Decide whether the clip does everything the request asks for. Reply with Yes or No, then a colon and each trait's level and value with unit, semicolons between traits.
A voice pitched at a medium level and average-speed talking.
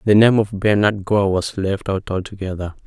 No: low, 100 Hz; average, 190 wpm